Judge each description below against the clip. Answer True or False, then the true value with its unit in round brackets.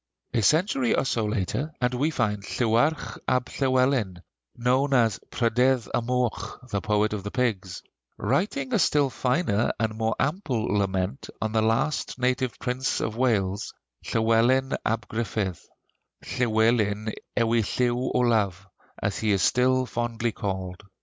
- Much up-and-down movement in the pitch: False (3.3 semitones)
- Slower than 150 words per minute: True (140 wpm)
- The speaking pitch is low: True (115 Hz)